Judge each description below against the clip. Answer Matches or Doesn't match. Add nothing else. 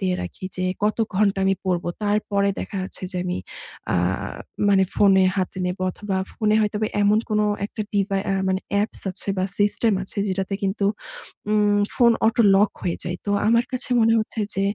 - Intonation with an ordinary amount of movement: Doesn't match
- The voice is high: Matches